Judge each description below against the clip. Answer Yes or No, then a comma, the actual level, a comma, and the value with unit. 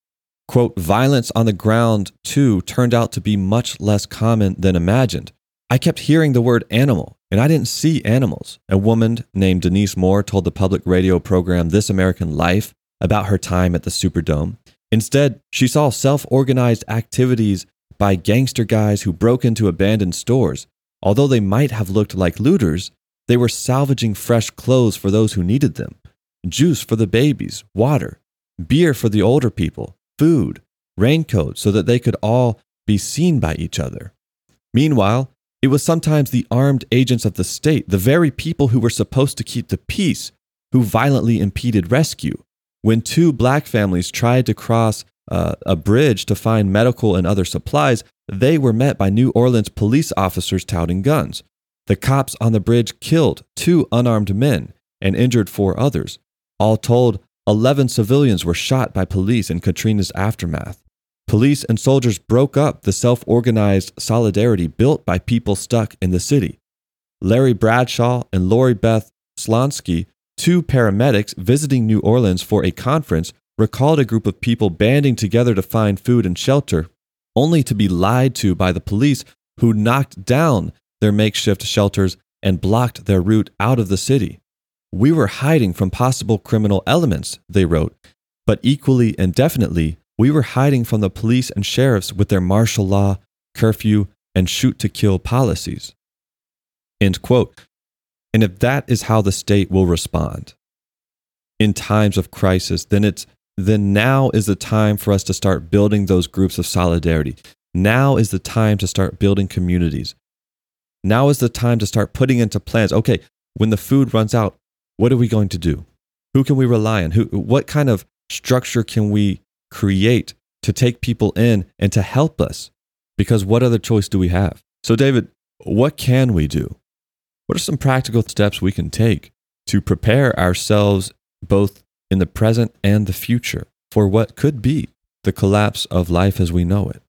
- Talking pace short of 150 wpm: No, average, 170 wpm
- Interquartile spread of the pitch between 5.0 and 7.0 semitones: No, average, 4.4 semitones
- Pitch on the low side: Yes, low, 110 Hz